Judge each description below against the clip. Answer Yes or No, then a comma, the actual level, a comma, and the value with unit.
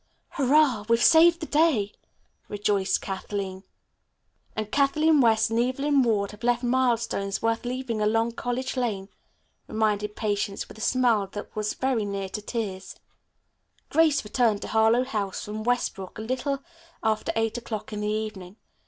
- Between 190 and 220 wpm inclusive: No, average, 155 wpm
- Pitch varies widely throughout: No, average, 3.5 semitones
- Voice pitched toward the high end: Yes, high, 225 Hz